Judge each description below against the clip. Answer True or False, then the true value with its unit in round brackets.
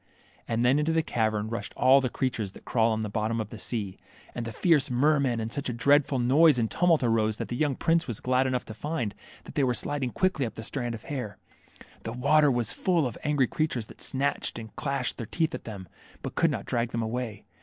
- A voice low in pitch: True (125 Hz)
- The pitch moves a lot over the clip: False (4.0 semitones)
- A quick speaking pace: True (235 wpm)